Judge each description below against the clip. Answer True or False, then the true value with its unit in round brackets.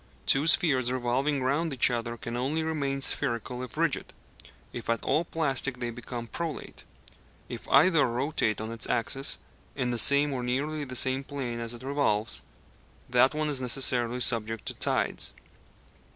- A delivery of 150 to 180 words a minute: True (160 wpm)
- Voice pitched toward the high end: False (130 Hz)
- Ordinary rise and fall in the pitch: True (3.0 semitones)